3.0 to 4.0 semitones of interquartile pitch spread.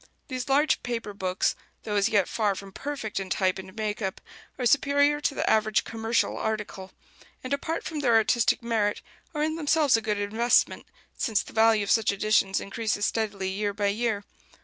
Yes: average, 3.4 semitones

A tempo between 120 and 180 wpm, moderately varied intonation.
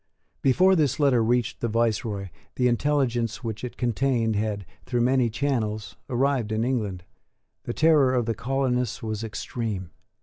Yes: average, 145 wpm; average, 3.2 semitones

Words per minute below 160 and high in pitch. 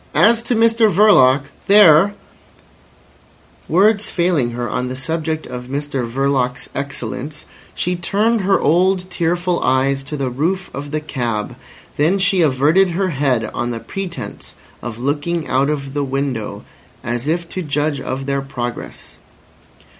No: average, 140 wpm; medium, 145 Hz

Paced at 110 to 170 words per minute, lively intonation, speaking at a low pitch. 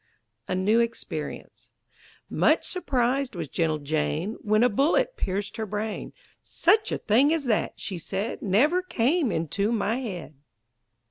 No: average, 140 wpm; wide, 6.0 semitones; high, 220 Hz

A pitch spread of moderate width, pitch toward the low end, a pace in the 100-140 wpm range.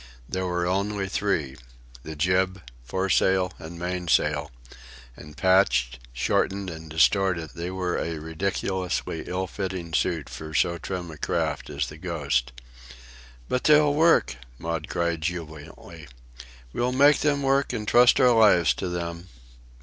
Yes: average, 3.5 semitones; very low, 90 Hz; slow, 135 wpm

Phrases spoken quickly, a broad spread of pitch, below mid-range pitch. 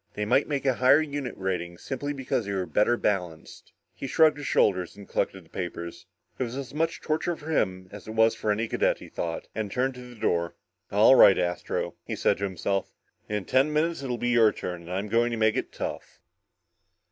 Yes: fast, 215 wpm; wide, 5.8 semitones; low, 110 Hz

